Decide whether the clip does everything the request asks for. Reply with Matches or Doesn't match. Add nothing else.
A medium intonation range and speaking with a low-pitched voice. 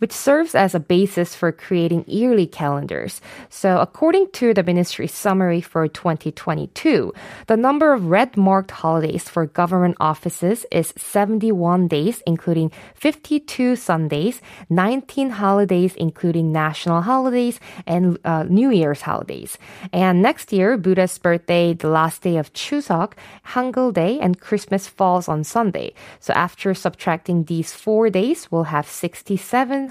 Doesn't match